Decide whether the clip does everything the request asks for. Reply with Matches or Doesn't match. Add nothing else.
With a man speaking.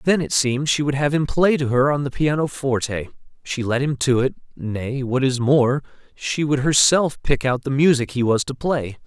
Matches